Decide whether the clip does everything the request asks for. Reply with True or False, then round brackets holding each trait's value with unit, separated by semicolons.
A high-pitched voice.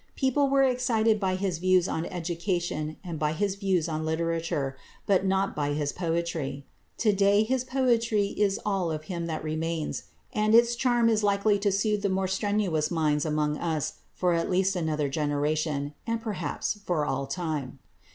False (180 Hz)